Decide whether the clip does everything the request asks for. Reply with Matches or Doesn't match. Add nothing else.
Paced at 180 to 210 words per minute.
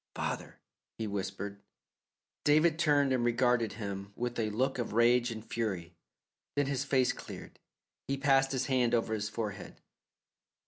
Doesn't match